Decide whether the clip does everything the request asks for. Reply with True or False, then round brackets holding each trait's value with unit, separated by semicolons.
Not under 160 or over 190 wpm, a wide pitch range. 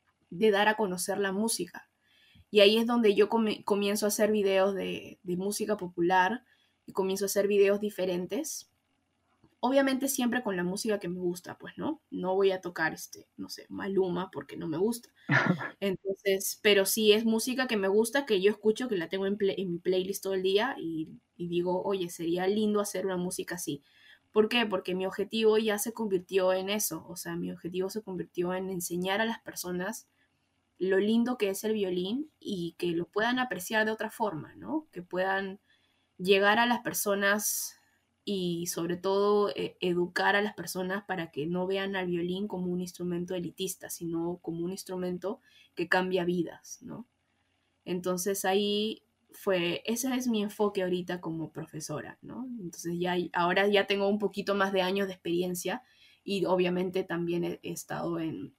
False (185 wpm; 2.7 semitones)